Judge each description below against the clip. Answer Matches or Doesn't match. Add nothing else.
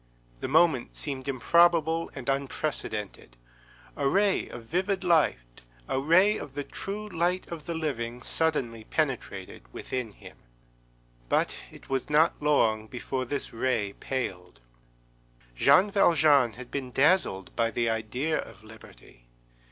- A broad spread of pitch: Matches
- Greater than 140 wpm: Doesn't match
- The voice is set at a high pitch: Doesn't match